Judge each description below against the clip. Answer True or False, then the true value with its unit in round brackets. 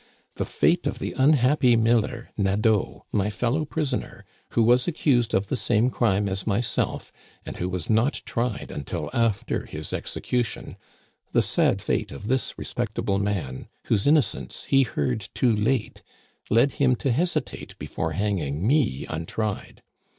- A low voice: True (115 Hz)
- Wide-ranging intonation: False (4.1 semitones)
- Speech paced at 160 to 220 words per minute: False (145 wpm)